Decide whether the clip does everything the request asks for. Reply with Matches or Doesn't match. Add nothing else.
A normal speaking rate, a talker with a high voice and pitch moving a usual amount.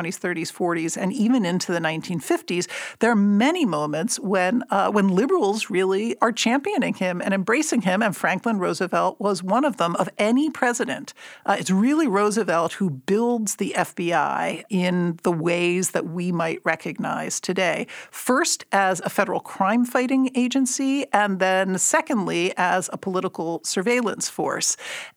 Matches